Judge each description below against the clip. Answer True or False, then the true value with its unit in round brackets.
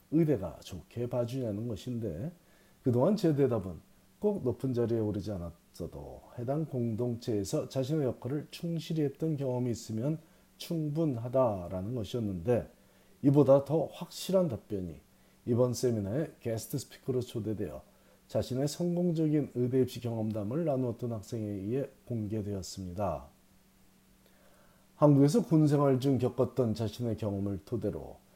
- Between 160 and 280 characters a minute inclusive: False (305 characters per minute)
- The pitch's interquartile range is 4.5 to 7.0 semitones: True (5.2 semitones)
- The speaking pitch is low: True (125 Hz)